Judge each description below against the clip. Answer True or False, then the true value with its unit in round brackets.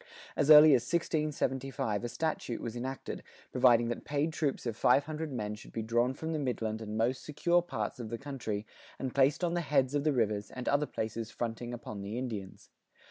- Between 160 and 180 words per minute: False (200 wpm)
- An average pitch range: True (4.3 semitones)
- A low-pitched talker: True (125 Hz)